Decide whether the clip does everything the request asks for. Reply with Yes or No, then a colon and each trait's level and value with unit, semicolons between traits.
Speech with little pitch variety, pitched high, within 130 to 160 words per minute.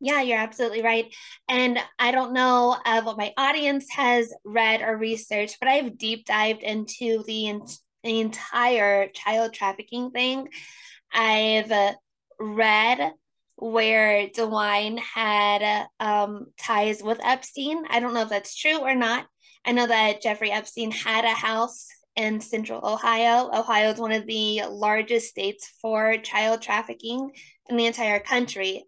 Yes: narrow, 2.2 semitones; high, 225 Hz; average, 145 wpm